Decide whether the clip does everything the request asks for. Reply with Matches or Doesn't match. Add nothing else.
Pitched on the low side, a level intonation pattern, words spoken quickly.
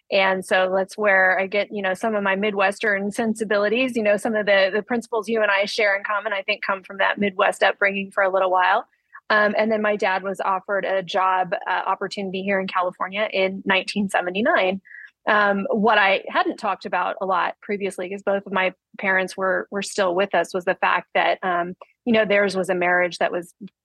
Doesn't match